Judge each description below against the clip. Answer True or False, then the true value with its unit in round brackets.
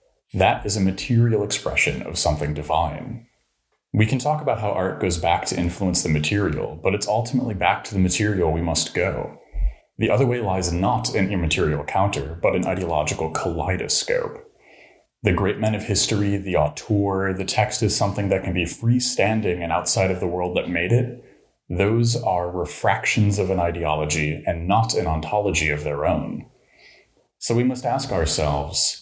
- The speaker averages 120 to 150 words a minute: False (170 wpm)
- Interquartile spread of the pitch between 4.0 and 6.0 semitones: True (4.3 semitones)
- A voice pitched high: False (100 Hz)